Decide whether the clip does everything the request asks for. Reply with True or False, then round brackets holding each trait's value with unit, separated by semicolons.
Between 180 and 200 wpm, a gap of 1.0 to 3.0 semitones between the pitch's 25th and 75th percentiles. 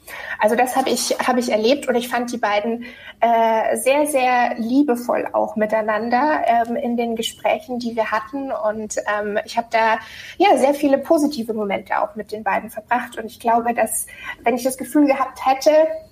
False (185 wpm; 3.7 semitones)